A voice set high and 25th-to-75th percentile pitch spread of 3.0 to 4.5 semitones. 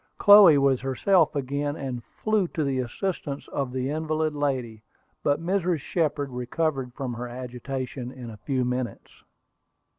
No: medium, 140 Hz; average, 3.8 semitones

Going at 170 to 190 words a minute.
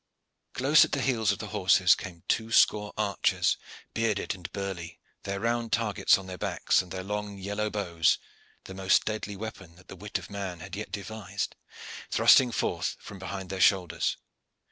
Yes: average, 175 wpm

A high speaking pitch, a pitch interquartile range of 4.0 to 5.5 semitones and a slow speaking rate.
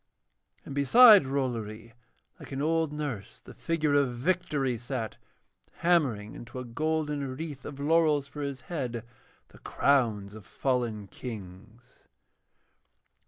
No: low, 135 Hz; average, 4.4 semitones; slow, 120 wpm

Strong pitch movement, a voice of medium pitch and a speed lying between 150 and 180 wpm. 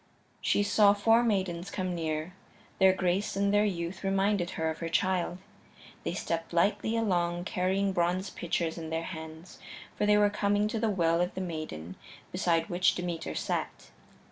No: average, 3.1 semitones; medium, 180 Hz; average, 170 wpm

